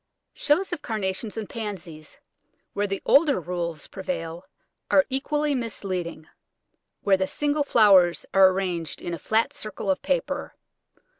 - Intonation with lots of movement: Yes, wide, 6.8 semitones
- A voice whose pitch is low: No, high, 195 Hz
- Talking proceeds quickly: No, slow, 135 wpm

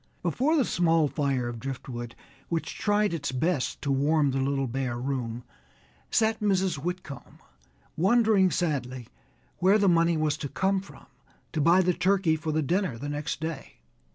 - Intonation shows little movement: No, wide, 5.4 semitones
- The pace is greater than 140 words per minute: Yes, average, 160 wpm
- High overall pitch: No, medium, 155 Hz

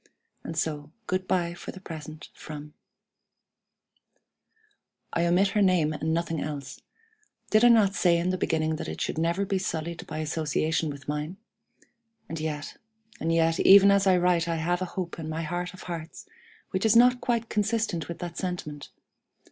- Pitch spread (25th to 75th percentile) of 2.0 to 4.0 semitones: Yes, average, 3.0 semitones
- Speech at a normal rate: Yes, average, 180 wpm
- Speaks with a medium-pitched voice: Yes, medium, 170 Hz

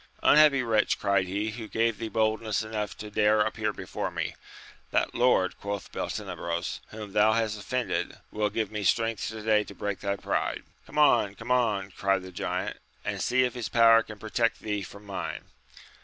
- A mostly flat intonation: Yes, narrow, 2.0 semitones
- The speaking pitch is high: No, low, 110 Hz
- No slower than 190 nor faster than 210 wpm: Yes, average, 195 wpm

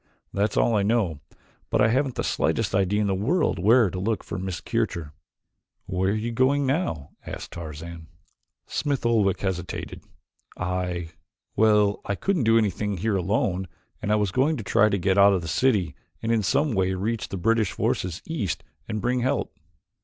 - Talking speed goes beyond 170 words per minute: Yes, average, 185 wpm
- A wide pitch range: No, average, 3.8 semitones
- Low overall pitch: Yes, low, 100 Hz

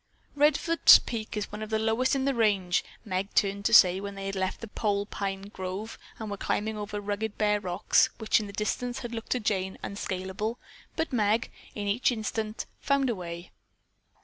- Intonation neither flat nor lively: No, narrow, 2.3 semitones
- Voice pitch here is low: No, high, 210 Hz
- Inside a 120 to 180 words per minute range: No, average, 195 wpm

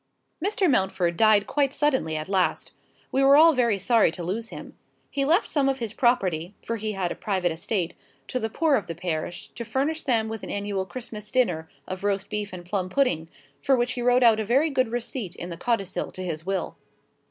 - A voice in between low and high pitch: No, high, 215 Hz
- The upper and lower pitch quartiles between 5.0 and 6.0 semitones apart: Yes, wide, 5.5 semitones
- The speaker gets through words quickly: Yes, fast, 215 wpm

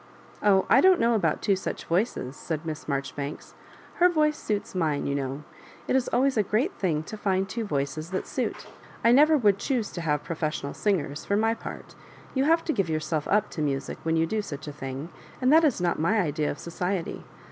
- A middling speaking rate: No, fast, 210 wpm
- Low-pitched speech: No, medium, 185 Hz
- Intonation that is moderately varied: No, wide, 6.8 semitones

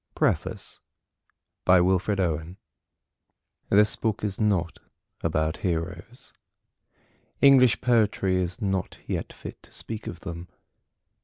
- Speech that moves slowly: Yes, slow, 95 wpm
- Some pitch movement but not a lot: Yes, average, 3.6 semitones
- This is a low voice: Yes, very low, 95 Hz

